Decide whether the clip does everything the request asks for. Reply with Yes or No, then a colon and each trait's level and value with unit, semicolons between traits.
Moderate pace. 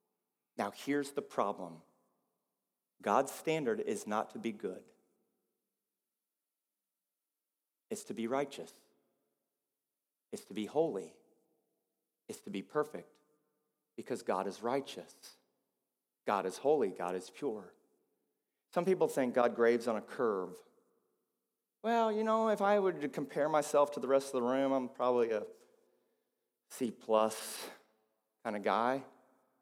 No: slow, 130 wpm